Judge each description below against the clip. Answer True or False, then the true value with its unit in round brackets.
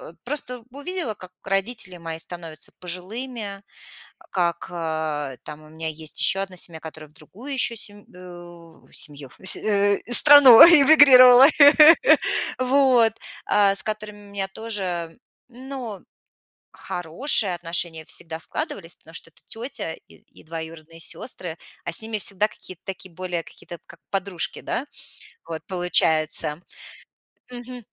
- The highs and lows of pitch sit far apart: True (5.7 semitones)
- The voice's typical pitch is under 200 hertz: True (185 Hz)